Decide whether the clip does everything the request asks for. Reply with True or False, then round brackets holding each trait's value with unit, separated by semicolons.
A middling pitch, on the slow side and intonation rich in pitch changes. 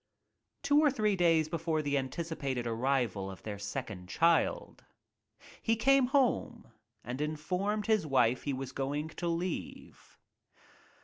True (155 Hz; 130 wpm; 7.4 semitones)